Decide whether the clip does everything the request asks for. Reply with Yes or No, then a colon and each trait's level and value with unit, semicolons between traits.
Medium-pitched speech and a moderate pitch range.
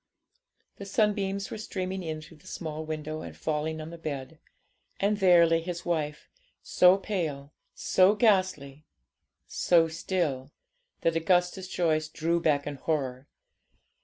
Yes: medium, 165 Hz; average, 3.3 semitones